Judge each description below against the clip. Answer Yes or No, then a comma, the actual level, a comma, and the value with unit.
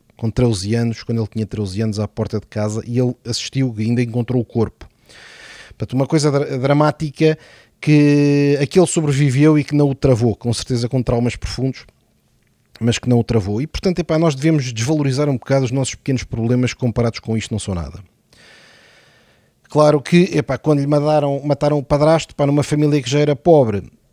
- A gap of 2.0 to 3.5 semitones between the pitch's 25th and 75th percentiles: No, average, 4.2 semitones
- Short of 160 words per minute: No, fast, 185 wpm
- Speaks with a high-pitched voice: No, low, 130 Hz